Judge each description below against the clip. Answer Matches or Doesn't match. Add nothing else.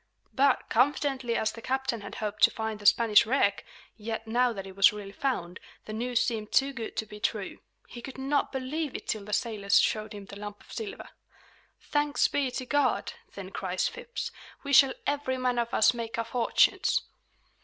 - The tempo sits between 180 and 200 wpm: Matches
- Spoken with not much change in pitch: Doesn't match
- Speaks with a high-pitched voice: Matches